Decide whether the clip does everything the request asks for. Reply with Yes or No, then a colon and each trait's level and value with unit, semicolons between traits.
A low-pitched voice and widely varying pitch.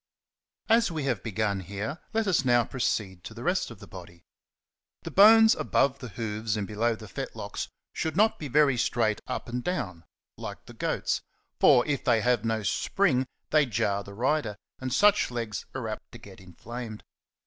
Yes: low, 120 Hz; wide, 6.0 semitones